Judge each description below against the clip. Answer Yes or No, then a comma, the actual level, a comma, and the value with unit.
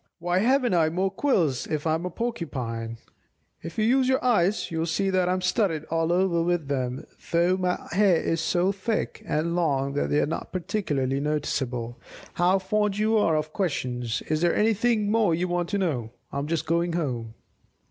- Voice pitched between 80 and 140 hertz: No, medium, 170 Hz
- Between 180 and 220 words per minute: Yes, average, 190 wpm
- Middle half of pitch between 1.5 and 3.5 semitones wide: No, average, 4.4 semitones